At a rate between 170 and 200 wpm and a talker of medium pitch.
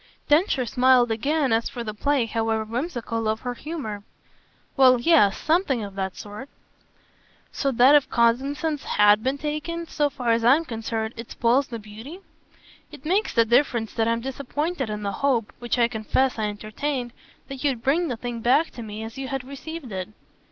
No: average, 180 wpm; high, 245 Hz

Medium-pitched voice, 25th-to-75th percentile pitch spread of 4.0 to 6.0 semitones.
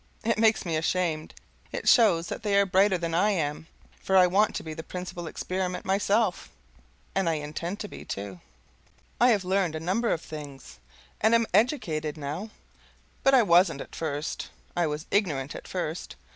Yes: medium, 180 Hz; average, 4.4 semitones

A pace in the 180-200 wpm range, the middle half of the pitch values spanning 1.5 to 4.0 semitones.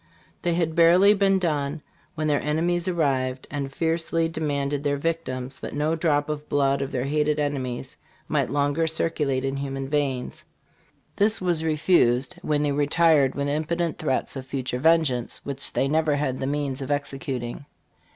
No: average, 160 wpm; average, 3.0 semitones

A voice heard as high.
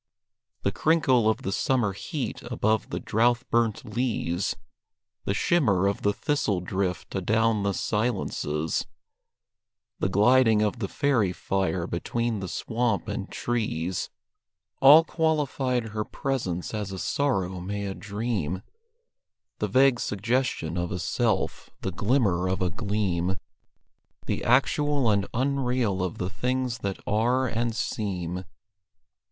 No: low, 110 Hz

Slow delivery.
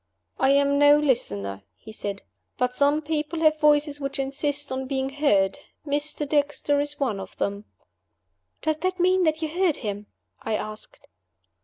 No: average, 160 wpm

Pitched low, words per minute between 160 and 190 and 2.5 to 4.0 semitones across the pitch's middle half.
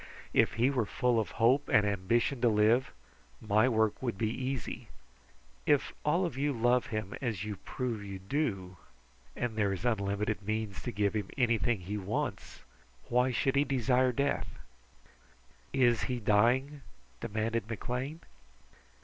No: low, 115 Hz; average, 150 wpm; average, 3.5 semitones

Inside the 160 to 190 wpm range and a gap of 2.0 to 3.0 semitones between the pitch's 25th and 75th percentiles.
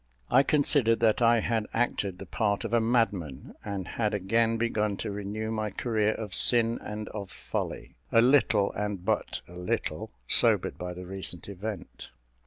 Yes: average, 170 wpm; narrow, 2.5 semitones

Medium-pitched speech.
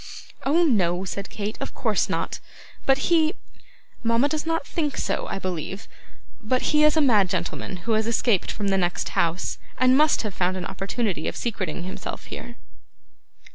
No: high, 220 Hz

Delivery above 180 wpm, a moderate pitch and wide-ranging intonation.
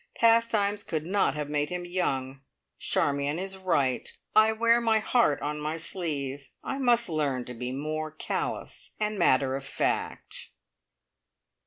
No: average, 145 wpm; medium, 155 Hz; wide, 6.8 semitones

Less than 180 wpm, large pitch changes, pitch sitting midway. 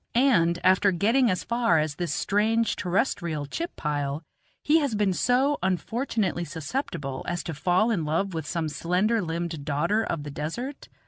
Yes: average, 160 wpm; wide, 6.0 semitones; medium, 180 Hz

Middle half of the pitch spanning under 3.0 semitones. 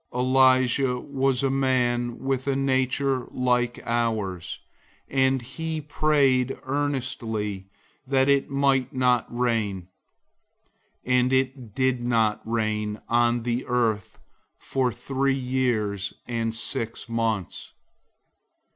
Yes: narrow, 2.5 semitones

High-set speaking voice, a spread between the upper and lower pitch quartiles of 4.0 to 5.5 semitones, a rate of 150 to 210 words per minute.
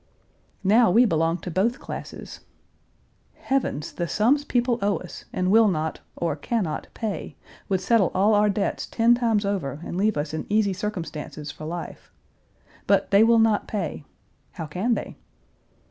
Yes: high, 200 Hz; average, 4.9 semitones; average, 160 wpm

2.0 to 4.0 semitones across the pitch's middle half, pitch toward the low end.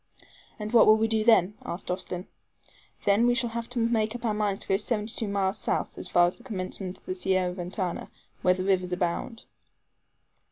No: average, 3.5 semitones; high, 200 Hz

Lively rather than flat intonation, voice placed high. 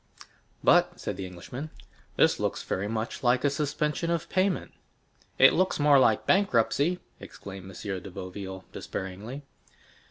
No: wide, 7.7 semitones; low, 120 Hz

